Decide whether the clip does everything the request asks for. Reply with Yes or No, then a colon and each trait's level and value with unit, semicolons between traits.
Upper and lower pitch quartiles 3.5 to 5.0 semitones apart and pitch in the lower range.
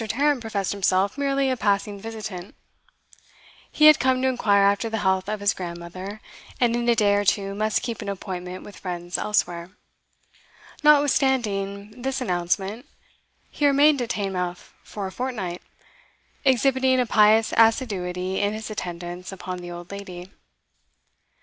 No: average, 4.6 semitones; high, 205 Hz